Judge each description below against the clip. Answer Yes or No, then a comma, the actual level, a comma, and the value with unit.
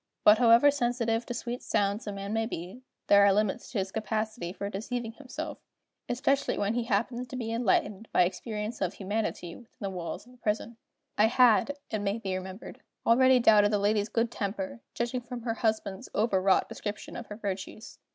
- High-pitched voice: Yes, high, 220 Hz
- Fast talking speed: No, average, 190 wpm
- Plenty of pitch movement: No, average, 3.1 semitones